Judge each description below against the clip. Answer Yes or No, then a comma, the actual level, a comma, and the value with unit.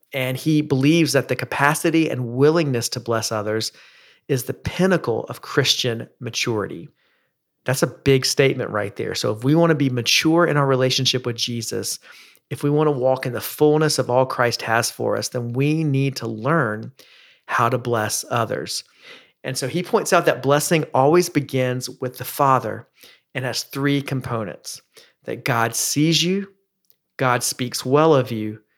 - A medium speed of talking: Yes, average, 175 wpm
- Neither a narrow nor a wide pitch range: Yes, average, 3.6 semitones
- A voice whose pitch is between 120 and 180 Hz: Yes, low, 135 Hz